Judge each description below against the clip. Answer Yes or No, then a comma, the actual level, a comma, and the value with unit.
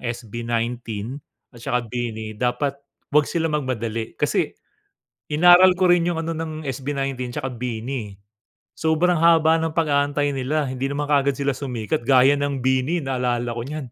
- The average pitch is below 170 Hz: Yes, low, 135 Hz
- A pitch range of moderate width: Yes, average, 4.0 semitones